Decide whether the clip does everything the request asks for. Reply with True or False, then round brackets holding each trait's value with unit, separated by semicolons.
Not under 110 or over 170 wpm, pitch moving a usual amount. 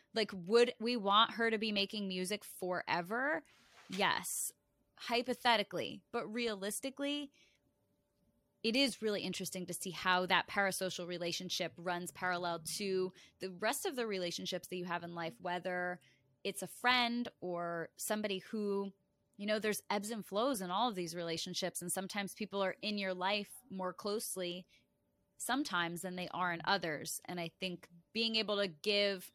True (155 wpm; 3.5 semitones)